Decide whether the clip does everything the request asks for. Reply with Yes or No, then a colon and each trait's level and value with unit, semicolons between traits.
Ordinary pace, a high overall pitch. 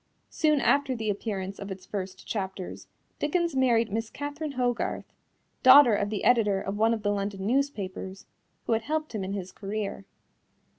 Yes: average, 165 wpm; high, 220 Hz